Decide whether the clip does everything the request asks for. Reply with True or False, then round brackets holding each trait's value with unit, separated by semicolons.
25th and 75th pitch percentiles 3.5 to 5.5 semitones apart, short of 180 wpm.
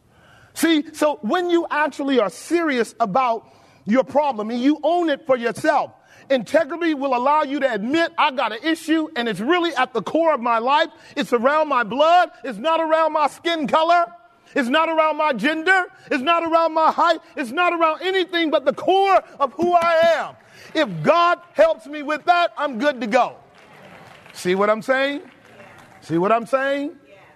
False (3.9 semitones; 185 wpm)